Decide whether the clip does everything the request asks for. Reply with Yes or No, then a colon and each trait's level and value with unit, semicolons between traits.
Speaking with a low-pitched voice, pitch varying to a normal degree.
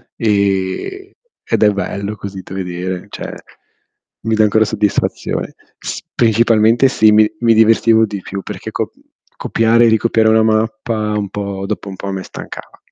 No: low, 110 Hz; narrow, 2.0 semitones